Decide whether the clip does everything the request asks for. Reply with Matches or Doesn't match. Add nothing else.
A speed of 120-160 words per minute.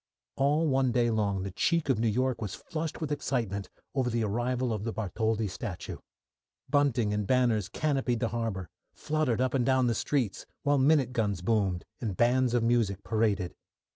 Doesn't match